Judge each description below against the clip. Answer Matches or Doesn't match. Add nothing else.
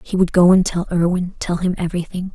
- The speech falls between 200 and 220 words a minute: Matches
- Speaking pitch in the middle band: Matches